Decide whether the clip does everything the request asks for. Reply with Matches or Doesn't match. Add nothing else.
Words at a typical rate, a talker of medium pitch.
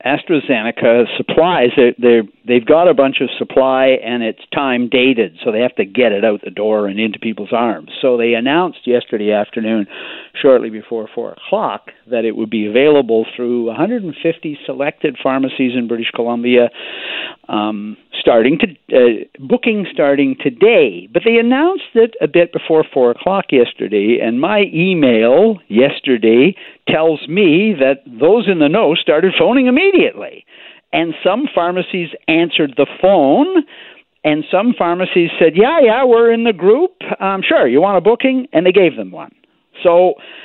Matches